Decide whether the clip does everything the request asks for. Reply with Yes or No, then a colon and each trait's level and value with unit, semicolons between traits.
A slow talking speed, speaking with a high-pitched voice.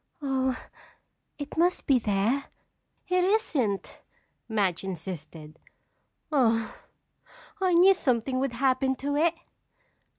Yes: slow, 100 wpm; very high, 260 Hz